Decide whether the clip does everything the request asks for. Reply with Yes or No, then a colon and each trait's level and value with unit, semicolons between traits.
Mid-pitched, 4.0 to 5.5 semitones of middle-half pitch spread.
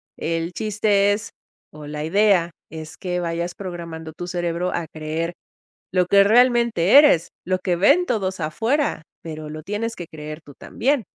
Yes: medium, 175 Hz; average, 4.3 semitones